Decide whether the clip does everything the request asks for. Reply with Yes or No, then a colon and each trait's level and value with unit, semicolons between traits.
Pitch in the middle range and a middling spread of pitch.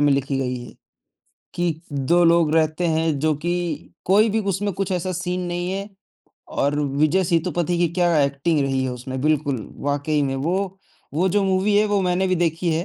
Yes: medium, 170 Hz; average, 4.1 semitones